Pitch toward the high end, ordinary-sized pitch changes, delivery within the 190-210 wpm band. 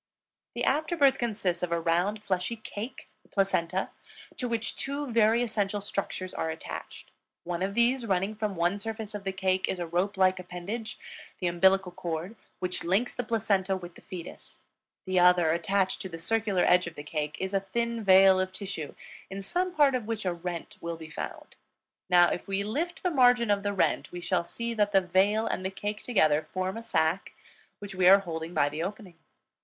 Yes: high, 195 Hz; average, 3.5 semitones; average, 200 wpm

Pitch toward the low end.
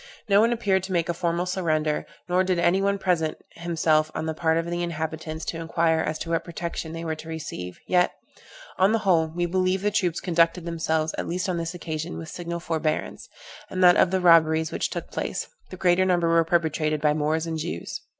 No: medium, 170 Hz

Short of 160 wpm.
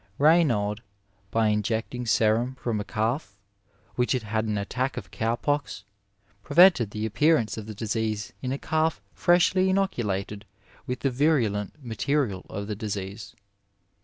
Yes: average, 140 wpm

